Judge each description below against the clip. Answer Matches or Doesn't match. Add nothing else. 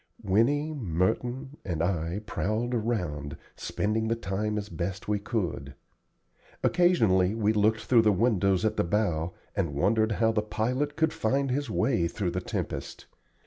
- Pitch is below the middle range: Matches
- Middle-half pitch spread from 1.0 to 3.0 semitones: Doesn't match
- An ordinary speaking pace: Matches